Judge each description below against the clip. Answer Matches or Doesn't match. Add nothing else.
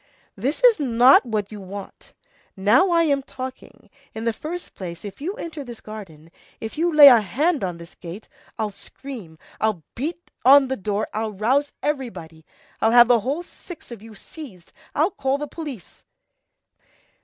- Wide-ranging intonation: Matches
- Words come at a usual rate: Matches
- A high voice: Matches